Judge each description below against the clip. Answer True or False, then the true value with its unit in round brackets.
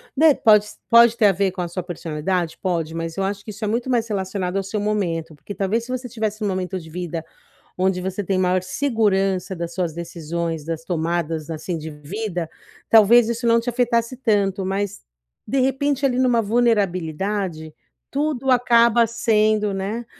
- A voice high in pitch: True (195 Hz)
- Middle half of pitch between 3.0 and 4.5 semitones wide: False (4.9 semitones)